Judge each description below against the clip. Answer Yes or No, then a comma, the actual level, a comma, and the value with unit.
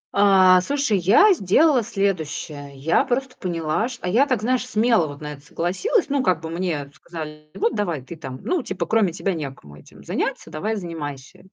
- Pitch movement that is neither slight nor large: No, wide, 6.9 semitones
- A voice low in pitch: No, medium, 180 Hz